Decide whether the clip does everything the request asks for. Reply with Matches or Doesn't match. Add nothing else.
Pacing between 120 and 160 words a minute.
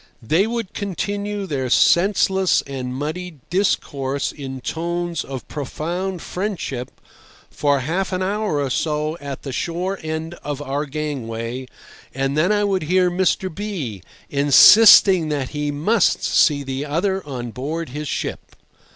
Matches